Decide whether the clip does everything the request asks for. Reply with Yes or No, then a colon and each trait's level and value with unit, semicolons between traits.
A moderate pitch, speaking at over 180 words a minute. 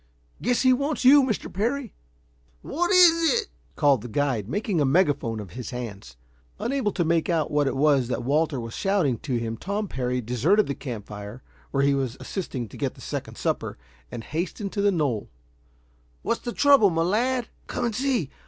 Yes: medium, 155 Hz; average, 190 wpm